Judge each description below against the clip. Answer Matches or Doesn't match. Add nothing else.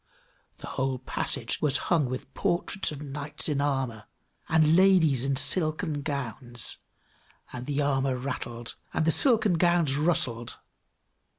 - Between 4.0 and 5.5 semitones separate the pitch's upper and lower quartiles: Doesn't match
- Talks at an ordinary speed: Doesn't match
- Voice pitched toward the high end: Doesn't match